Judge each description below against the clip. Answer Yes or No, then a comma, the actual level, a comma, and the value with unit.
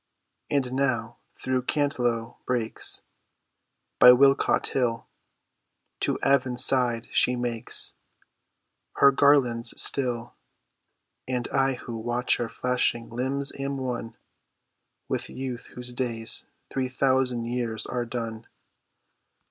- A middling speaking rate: No, slow, 105 wpm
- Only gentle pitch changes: Yes, narrow, 2.0 semitones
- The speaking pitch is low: Yes, low, 125 Hz